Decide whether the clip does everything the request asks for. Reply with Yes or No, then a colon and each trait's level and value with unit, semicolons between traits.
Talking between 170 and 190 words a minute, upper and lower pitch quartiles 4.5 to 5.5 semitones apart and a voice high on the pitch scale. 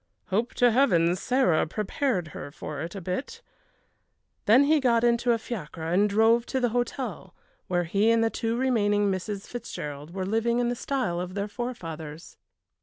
Yes: average, 175 wpm; average, 5.2 semitones; high, 215 Hz